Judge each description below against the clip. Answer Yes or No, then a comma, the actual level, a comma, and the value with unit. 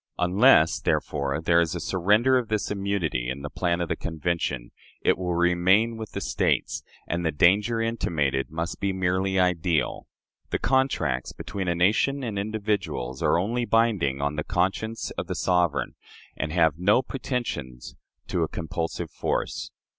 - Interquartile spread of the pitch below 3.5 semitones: No, average, 4.8 semitones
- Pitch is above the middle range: No, very low, 90 Hz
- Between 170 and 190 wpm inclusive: No, average, 160 wpm